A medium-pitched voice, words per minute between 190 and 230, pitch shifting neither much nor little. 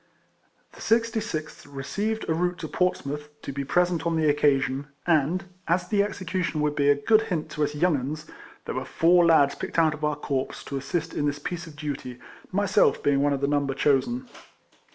Yes: medium, 155 Hz; average, 195 wpm; average, 3.8 semitones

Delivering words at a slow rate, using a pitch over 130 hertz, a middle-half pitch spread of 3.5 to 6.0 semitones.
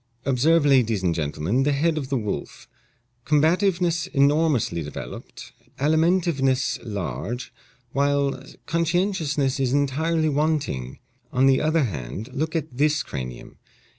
Yes: slow, 115 wpm; medium, 140 Hz; average, 4.5 semitones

